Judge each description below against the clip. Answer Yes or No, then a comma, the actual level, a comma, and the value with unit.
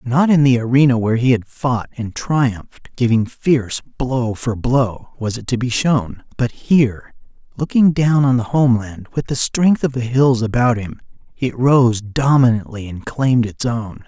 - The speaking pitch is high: No, low, 120 Hz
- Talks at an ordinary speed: Yes, average, 180 wpm